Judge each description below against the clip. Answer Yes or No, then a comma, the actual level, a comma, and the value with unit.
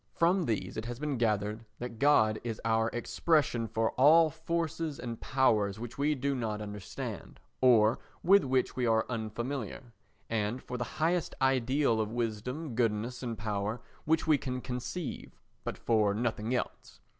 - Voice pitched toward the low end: Yes, low, 120 Hz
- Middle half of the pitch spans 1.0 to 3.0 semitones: No, average, 4.1 semitones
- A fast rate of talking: No, average, 155 wpm